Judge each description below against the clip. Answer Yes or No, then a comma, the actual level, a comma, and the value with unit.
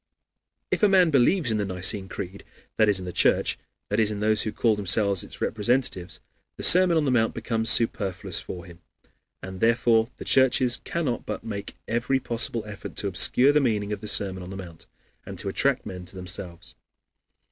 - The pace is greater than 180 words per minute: Yes, average, 195 wpm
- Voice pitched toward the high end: No, low, 105 Hz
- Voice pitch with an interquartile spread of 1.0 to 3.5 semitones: No, average, 4.0 semitones